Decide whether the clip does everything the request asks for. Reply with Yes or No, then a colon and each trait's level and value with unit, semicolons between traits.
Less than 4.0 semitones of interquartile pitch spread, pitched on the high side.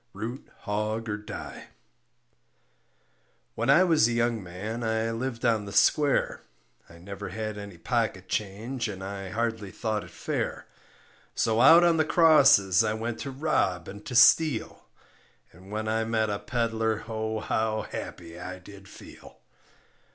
No: narrow, 2.6 semitones; low, 110 Hz